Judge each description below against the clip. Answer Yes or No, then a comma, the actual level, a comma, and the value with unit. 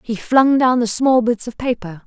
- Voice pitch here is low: No, high, 235 Hz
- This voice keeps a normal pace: No, fast, 230 wpm